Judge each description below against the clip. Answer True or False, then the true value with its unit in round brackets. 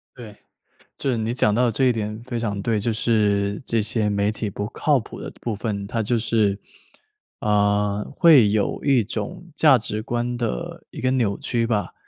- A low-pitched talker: True (110 Hz)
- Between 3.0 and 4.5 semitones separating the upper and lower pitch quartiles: False (2.6 semitones)